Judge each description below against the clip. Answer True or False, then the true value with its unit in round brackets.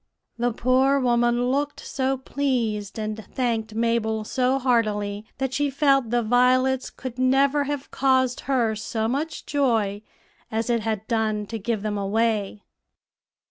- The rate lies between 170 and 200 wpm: False (145 wpm)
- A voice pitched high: True (240 Hz)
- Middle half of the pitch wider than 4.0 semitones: False (3.2 semitones)